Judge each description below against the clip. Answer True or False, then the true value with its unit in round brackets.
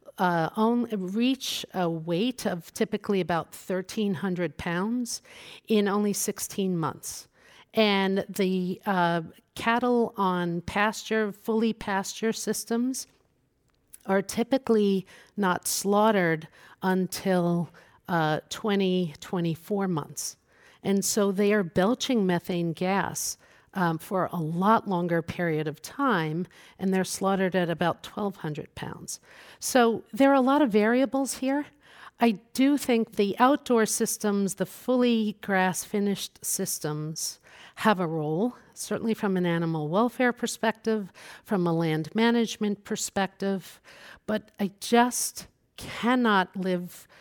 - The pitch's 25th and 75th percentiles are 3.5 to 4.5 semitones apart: True (3.9 semitones)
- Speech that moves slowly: True (115 wpm)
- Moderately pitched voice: False (195 Hz)